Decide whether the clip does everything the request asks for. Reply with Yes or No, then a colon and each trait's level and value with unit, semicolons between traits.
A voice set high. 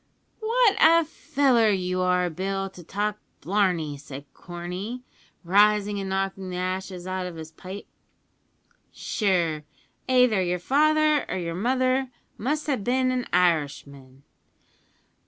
Yes: high, 195 Hz